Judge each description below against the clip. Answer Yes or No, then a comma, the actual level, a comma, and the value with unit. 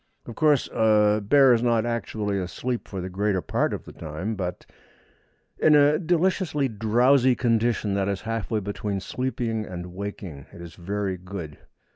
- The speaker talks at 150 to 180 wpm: Yes, average, 160 wpm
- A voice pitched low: Yes, low, 110 Hz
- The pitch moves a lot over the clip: No, average, 4.1 semitones